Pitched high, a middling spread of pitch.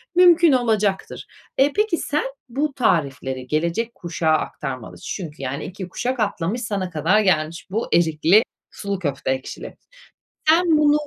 No: high, 195 Hz; wide, 8.4 semitones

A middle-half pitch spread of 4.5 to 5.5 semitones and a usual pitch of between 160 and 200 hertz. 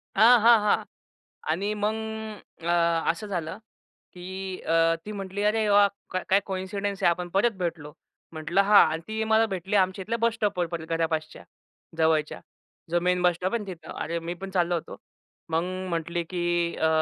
No: average, 3.3 semitones; medium, 185 Hz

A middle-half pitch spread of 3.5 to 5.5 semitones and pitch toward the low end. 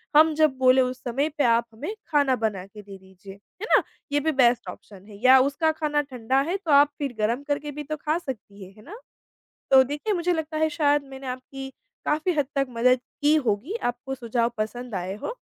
No: average, 4.3 semitones; very high, 265 Hz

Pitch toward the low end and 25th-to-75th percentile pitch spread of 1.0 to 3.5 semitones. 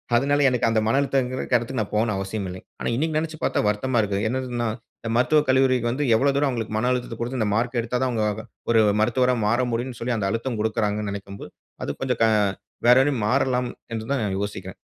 Yes: low, 120 Hz; average, 3.0 semitones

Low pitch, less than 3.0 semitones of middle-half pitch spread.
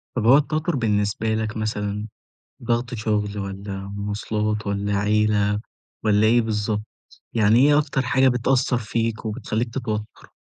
Yes: low, 110 Hz; narrow, 2.4 semitones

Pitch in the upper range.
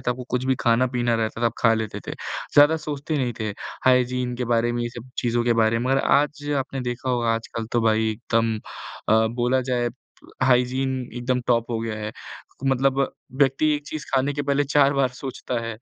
No: low, 125 Hz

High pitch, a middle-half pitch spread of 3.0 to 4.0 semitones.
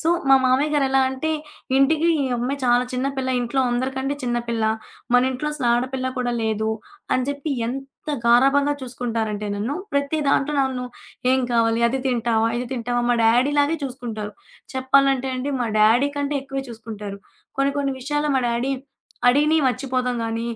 No: very high, 255 Hz; narrow, 2.6 semitones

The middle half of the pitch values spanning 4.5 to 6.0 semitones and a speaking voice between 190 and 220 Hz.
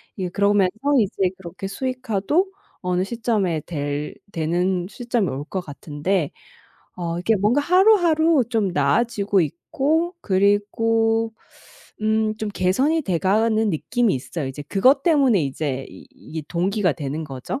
Yes: wide, 5.5 semitones; high, 200 Hz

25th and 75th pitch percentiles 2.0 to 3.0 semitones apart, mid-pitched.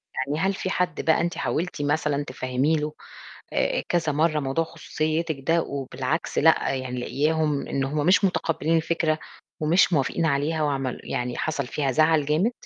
Yes: average, 2.7 semitones; medium, 155 Hz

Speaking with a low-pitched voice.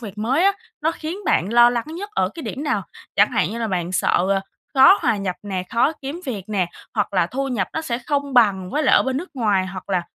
No: high, 235 Hz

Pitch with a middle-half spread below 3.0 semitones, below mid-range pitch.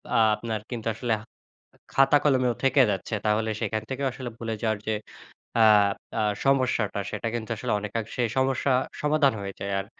No: average, 3.5 semitones; low, 120 Hz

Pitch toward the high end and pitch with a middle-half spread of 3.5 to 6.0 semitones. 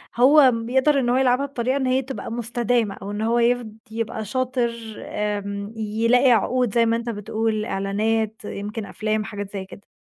No: high, 230 Hz; average, 2.8 semitones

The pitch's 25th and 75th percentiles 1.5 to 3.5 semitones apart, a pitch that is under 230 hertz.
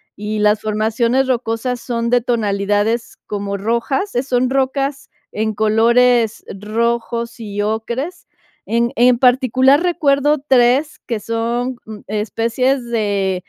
No: average, 3.0 semitones; high, 235 Hz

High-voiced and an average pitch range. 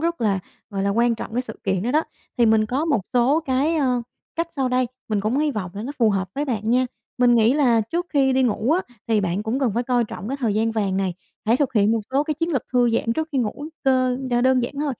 Yes: high, 245 Hz; average, 3.8 semitones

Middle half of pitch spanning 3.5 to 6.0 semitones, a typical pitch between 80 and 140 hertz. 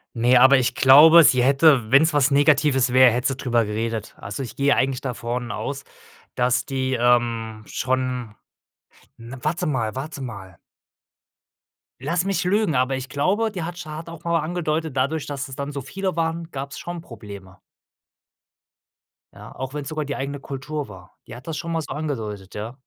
Yes: average, 4.3 semitones; low, 135 Hz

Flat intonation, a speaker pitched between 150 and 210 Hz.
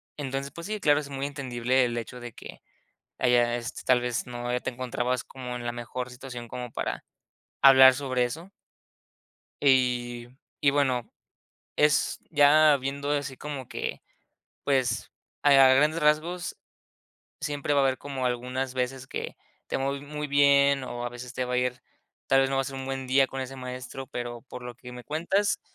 No: narrow, 2.3 semitones; low, 130 Hz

